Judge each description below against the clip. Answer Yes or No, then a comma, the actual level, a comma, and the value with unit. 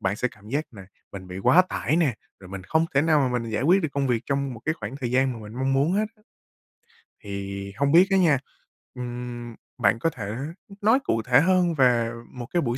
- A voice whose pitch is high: No, low, 125 Hz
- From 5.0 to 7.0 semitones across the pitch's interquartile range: Yes, wide, 5.6 semitones